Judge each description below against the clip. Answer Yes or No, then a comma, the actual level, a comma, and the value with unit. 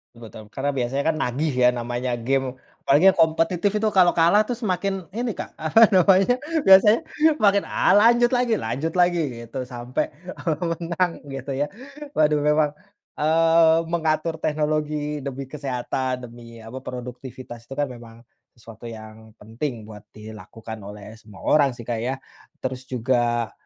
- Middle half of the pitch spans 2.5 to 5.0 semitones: No, wide, 5.6 semitones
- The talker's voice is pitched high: No, medium, 140 Hz